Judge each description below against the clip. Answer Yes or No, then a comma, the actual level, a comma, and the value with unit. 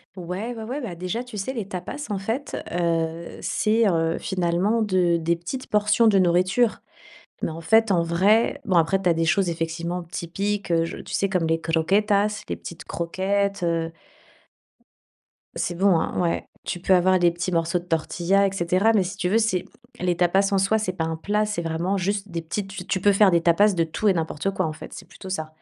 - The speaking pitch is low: No, medium, 185 Hz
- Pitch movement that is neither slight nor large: Yes, average, 3.2 semitones